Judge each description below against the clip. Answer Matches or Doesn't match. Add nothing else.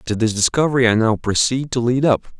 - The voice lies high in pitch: Doesn't match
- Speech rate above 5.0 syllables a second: Matches